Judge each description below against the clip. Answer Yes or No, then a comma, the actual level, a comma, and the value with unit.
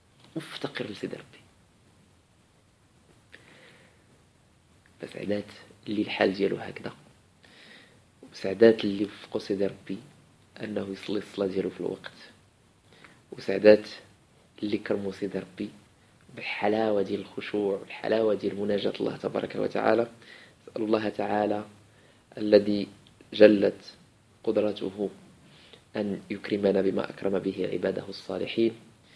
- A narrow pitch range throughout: Yes, narrow, 1.9 semitones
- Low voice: Yes, low, 105 Hz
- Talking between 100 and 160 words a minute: No, average, 90 wpm